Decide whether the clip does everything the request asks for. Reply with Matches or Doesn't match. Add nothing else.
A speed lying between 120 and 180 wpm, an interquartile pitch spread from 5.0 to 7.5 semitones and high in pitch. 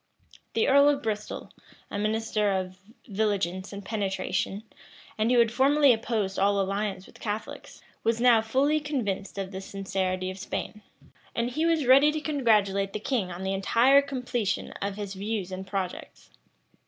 Doesn't match